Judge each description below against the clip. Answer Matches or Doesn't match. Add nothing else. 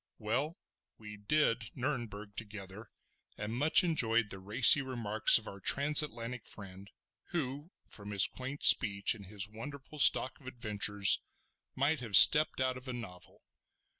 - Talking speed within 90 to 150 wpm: Matches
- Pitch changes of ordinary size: Matches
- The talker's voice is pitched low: Matches